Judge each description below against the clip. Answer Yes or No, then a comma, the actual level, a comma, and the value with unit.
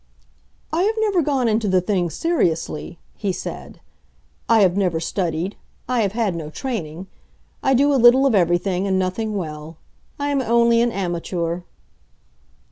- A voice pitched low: No, high, 200 Hz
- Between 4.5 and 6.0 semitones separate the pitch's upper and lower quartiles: Yes, wide, 5.6 semitones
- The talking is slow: No, average, 155 wpm